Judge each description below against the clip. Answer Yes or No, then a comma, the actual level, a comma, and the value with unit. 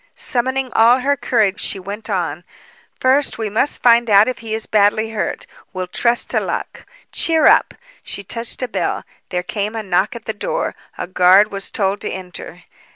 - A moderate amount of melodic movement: Yes, average, 3.7 semitones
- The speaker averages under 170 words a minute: No, average, 185 wpm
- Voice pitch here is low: No, high, 220 Hz